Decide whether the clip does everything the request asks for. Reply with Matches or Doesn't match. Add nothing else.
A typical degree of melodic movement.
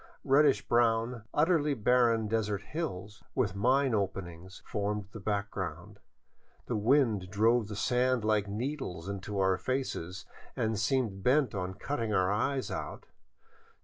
Matches